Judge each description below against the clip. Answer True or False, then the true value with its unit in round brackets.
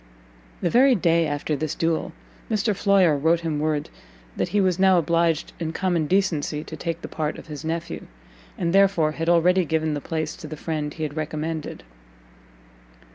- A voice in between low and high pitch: True (165 Hz)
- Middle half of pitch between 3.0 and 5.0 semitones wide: False (2.5 semitones)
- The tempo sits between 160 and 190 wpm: True (180 wpm)